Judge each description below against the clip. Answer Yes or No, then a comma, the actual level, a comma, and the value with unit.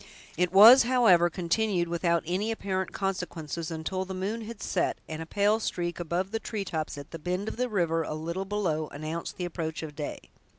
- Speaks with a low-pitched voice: No, medium, 180 Hz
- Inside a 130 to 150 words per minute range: No, average, 195 wpm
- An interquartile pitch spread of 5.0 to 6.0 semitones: No, average, 3.5 semitones